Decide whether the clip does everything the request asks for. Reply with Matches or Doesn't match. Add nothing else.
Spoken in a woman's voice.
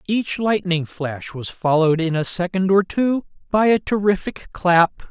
Doesn't match